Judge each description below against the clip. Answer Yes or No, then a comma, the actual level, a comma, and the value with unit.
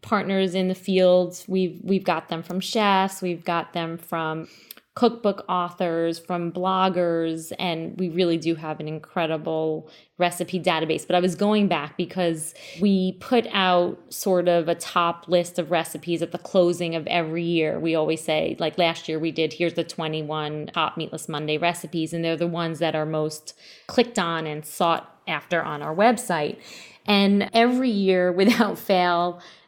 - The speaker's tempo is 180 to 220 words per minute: No, average, 170 wpm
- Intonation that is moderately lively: No, narrow, 2.3 semitones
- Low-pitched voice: No, medium, 175 Hz